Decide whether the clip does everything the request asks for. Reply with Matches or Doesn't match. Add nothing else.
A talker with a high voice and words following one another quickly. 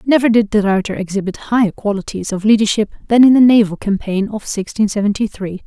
Doesn't match